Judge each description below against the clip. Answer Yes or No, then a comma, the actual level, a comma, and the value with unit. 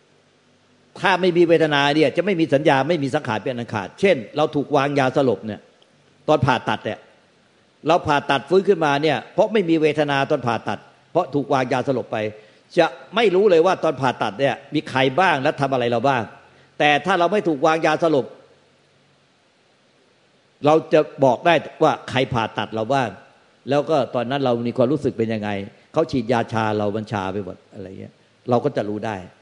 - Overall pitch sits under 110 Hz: No, medium, 140 Hz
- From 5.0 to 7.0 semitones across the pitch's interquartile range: Yes, wide, 5.6 semitones